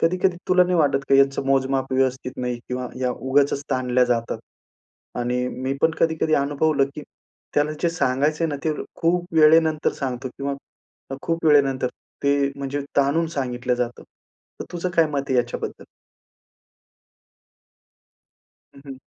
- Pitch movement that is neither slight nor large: Yes, average, 3.5 semitones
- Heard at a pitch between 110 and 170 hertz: Yes, medium, 140 Hz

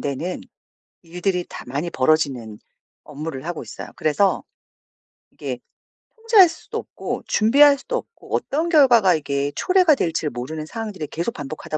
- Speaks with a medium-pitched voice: Yes, medium, 170 Hz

